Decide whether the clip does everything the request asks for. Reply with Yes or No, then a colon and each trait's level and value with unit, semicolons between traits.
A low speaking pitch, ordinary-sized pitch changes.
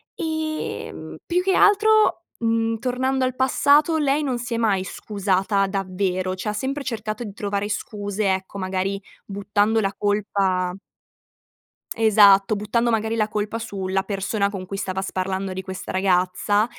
No: high, 205 Hz; average, 3.4 semitones